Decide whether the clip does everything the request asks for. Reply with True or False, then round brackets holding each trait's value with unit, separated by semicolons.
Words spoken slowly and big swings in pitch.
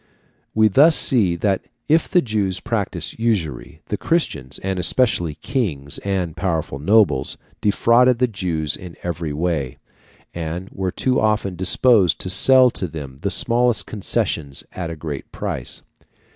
False (145 wpm; 5.8 semitones)